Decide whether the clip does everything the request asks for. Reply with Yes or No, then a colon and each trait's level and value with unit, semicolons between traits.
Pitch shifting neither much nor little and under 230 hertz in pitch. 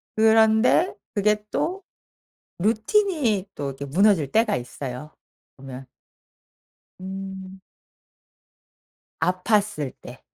No: wide, 6.7 semitones; high, 195 Hz